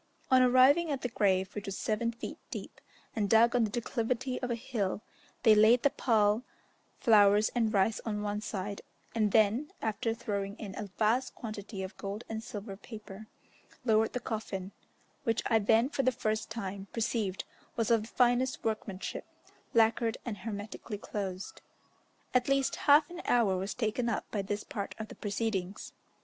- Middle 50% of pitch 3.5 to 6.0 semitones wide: No, narrow, 2.6 semitones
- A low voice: No, high, 220 Hz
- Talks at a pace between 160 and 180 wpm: Yes, average, 170 wpm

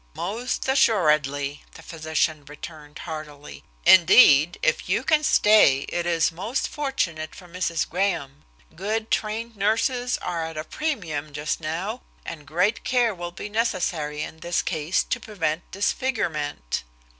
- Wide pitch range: Yes, wide, 5.8 semitones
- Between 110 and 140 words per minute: Yes, slow, 135 wpm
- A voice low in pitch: No, medium, 170 Hz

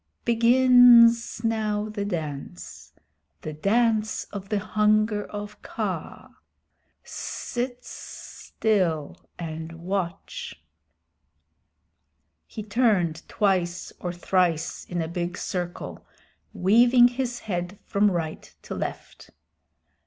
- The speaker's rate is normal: No, slow, 95 wpm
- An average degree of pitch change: Yes, average, 4.6 semitones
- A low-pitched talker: No, high, 205 Hz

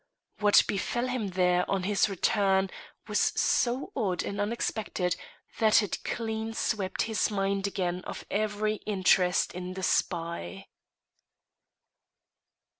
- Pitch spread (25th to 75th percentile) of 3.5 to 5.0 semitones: No, average, 2.8 semitones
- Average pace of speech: No, slow, 115 wpm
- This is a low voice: No, high, 200 Hz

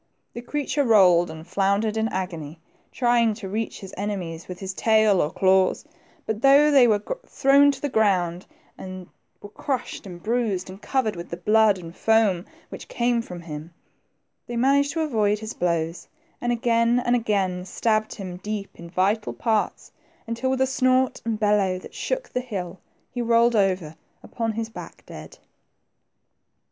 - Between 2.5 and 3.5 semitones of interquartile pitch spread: No, average, 4.4 semitones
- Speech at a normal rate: Yes, average, 170 wpm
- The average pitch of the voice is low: No, high, 215 Hz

